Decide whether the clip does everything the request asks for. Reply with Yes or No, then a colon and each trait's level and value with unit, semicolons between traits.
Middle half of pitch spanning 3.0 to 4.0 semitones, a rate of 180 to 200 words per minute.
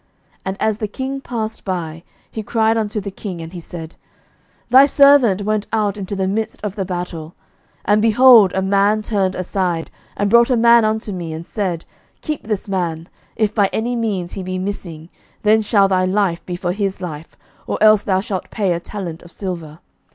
Yes: average, 3.3 semitones; average, 195 wpm